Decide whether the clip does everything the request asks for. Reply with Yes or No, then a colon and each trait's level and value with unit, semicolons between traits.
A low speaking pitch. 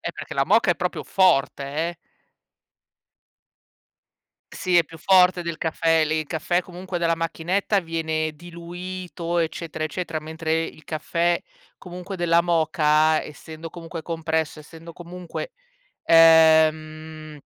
No: medium, 165 Hz